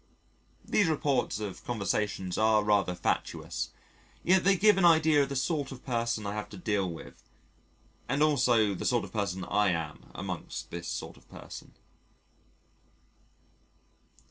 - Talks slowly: No, average, 145 wpm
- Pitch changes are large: Yes, wide, 6.3 semitones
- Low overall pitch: Yes, low, 110 Hz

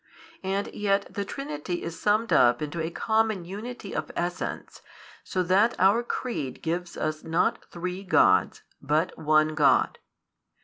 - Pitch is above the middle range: No, medium, 180 Hz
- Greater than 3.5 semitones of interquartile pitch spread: Yes, average, 4.6 semitones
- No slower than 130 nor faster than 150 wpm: Yes, average, 145 wpm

